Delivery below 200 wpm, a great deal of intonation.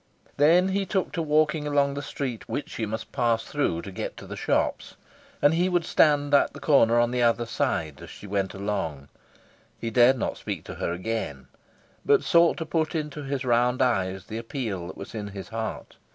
No: fast, 205 wpm; wide, 6.3 semitones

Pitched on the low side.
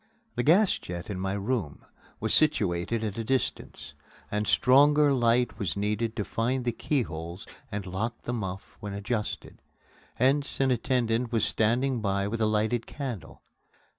Yes: low, 115 Hz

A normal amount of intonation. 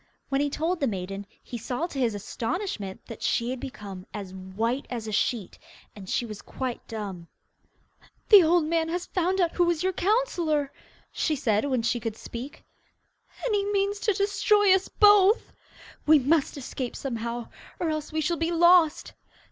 No: wide, 7.5 semitones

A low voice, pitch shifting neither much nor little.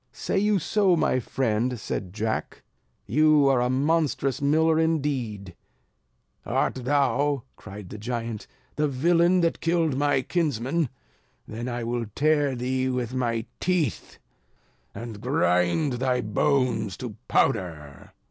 Yes: low, 130 Hz; average, 4.8 semitones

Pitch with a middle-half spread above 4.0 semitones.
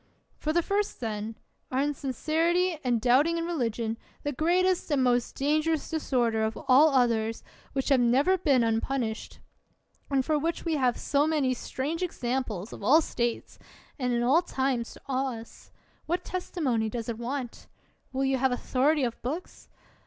Yes: average, 4.6 semitones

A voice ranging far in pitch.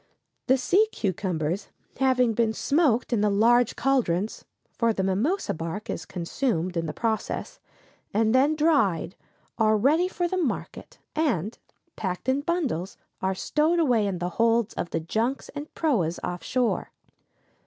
Yes: wide, 6.5 semitones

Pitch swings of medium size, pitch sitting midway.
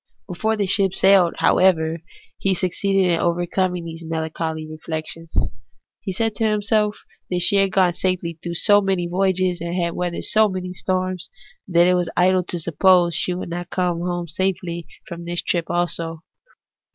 No: narrow, 1.9 semitones; medium, 180 Hz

